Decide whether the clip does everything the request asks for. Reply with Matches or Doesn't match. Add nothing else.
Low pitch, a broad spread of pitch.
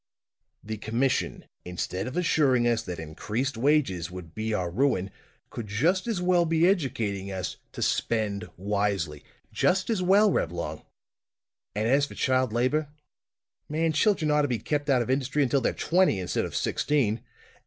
Matches